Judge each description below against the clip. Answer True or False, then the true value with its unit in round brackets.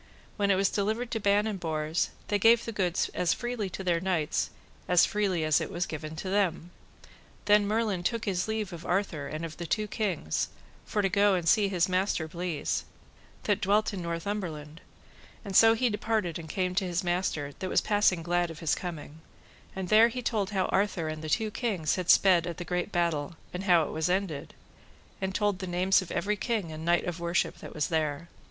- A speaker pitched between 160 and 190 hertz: True (185 Hz)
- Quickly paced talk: True (210 wpm)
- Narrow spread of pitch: False (3.6 semitones)